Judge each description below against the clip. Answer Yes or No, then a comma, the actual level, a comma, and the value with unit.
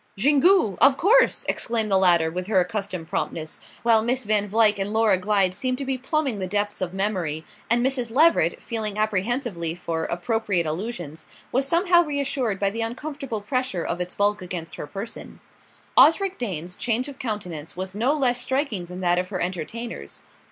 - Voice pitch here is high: Yes, high, 210 Hz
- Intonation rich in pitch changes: Yes, wide, 5.7 semitones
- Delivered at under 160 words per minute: No, average, 175 wpm